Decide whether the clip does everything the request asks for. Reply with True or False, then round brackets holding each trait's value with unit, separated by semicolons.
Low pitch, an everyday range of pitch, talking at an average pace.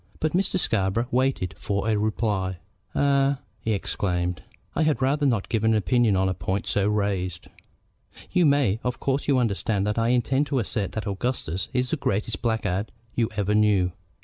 True (110 Hz; 4.7 semitones; 175 wpm)